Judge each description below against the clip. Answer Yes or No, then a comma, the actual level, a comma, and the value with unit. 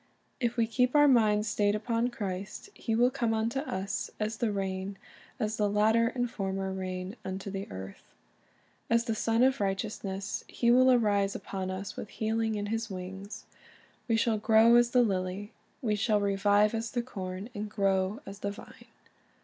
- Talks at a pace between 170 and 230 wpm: Yes, average, 180 wpm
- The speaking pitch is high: Yes, high, 210 Hz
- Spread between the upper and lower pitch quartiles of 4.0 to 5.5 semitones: No, average, 2.9 semitones